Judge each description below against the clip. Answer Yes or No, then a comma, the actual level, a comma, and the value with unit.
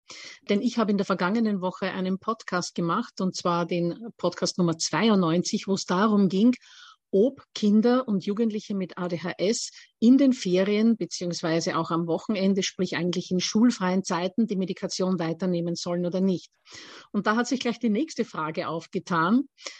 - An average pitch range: Yes, average, 4.0 semitones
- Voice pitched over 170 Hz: Yes, high, 190 Hz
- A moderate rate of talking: Yes, average, 160 wpm